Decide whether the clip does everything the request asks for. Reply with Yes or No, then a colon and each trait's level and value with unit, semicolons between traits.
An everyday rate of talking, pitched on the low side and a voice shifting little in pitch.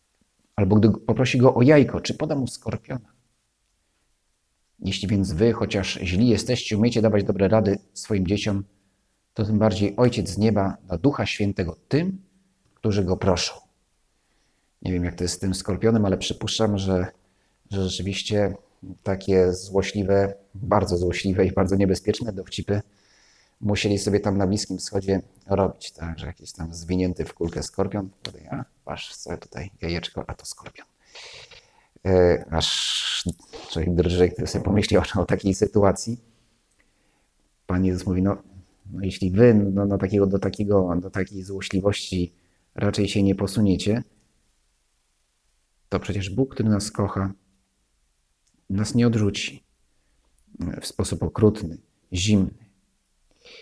Yes: average, 135 wpm; low, 100 Hz; narrow, 2.3 semitones